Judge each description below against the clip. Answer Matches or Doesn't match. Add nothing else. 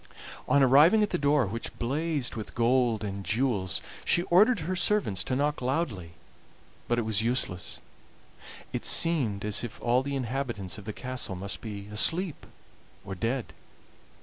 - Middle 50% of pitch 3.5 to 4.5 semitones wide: Doesn't match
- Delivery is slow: Doesn't match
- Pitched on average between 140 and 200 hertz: Doesn't match